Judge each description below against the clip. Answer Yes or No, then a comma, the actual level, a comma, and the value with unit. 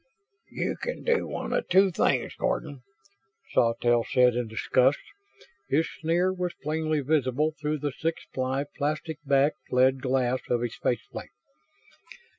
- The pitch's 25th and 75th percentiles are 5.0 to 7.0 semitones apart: No, average, 3.7 semitones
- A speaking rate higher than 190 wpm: No, average, 140 wpm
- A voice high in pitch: No, medium, 140 Hz